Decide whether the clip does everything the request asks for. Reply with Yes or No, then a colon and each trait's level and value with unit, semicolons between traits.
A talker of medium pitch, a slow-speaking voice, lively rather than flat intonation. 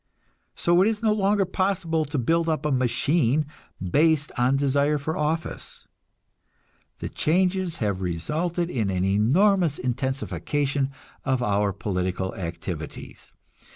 Yes: medium, 145 Hz; slow, 120 wpm; wide, 6.3 semitones